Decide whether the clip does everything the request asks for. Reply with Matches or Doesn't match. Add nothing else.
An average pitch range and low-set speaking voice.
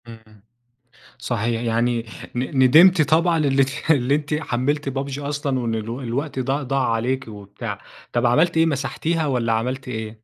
Matches